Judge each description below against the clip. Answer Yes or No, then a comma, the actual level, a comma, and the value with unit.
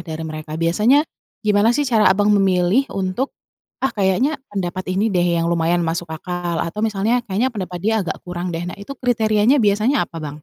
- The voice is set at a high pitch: Yes, high, 195 Hz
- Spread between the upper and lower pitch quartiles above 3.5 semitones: Yes, average, 4.1 semitones